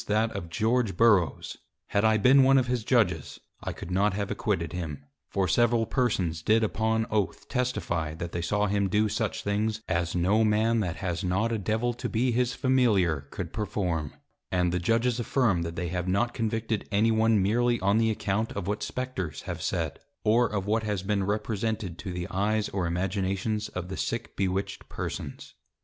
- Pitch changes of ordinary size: Yes, average, 3.6 semitones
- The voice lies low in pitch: Yes, low, 105 Hz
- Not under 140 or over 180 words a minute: No, average, 190 wpm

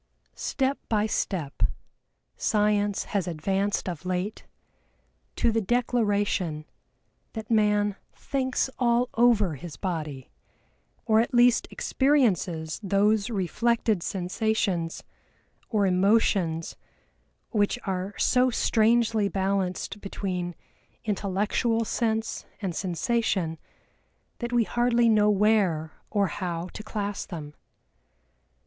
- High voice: Yes, high, 205 Hz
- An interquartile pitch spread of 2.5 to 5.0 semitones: Yes, average, 3.7 semitones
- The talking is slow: Yes, slow, 100 wpm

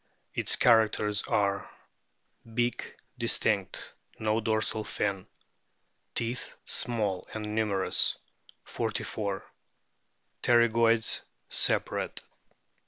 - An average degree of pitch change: No, narrow, 2.0 semitones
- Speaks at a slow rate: Yes, slow, 70 wpm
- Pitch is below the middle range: Yes, low, 110 Hz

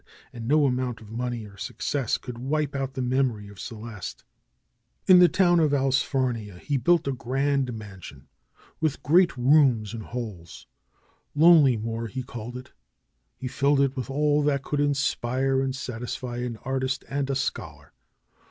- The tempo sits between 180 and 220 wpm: No, average, 155 wpm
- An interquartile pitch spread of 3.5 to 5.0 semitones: No, average, 3.1 semitones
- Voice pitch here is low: Yes, low, 130 Hz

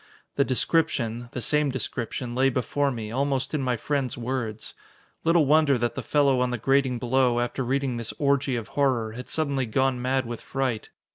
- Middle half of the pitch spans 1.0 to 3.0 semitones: Yes, narrow, 2.5 semitones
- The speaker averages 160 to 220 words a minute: Yes, average, 185 wpm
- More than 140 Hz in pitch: No, low, 130 Hz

